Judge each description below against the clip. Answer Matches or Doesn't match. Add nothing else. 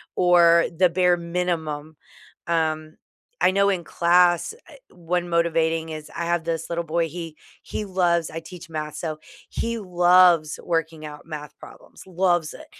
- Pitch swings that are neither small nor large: Doesn't match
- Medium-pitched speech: Matches